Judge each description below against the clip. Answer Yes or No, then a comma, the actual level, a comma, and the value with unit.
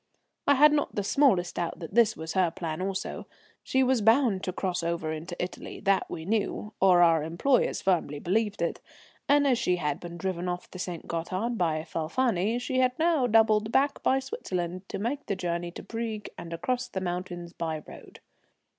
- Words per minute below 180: No, average, 190 wpm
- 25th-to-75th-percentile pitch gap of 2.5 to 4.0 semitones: No, wide, 5.4 semitones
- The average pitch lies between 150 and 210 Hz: Yes, high, 190 Hz